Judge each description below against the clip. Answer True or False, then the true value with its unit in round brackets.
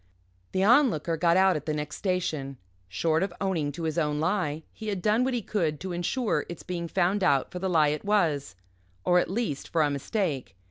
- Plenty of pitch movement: False (4.3 semitones)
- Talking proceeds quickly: True (215 wpm)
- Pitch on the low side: False (170 Hz)